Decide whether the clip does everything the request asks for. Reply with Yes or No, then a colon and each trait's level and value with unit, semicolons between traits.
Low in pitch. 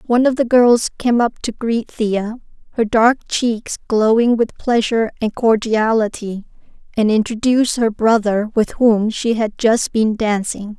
No: high, 225 Hz